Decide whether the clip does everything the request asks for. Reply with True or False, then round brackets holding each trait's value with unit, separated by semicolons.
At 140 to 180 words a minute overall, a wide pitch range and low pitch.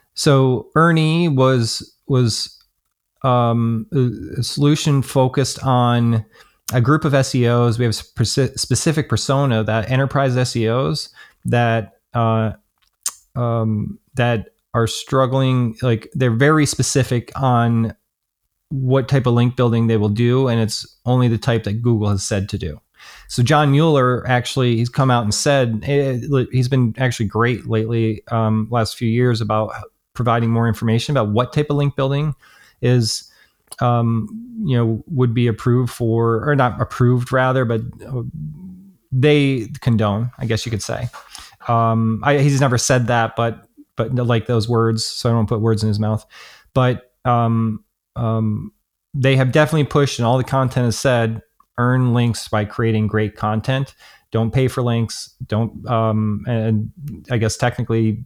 False (150 wpm; 2.7 semitones; 120 Hz)